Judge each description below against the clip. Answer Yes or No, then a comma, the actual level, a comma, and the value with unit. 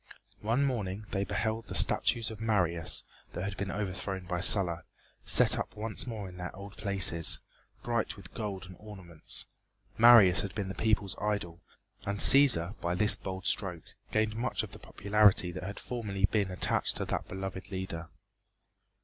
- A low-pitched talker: Yes, low, 100 Hz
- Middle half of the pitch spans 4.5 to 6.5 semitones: No, average, 2.7 semitones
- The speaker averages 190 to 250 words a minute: No, average, 165 wpm